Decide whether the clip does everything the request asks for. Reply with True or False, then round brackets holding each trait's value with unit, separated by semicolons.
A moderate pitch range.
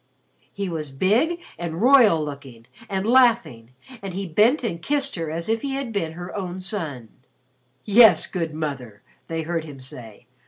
False (6.5 semitones)